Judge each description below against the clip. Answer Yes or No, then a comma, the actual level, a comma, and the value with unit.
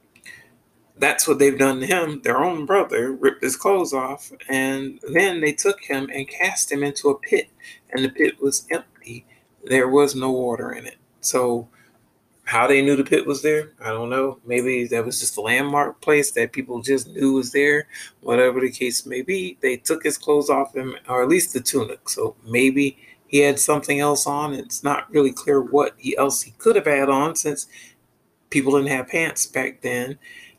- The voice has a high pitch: No, low, 135 Hz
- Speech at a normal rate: Yes, average, 195 wpm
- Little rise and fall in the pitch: Yes, narrow, 2.0 semitones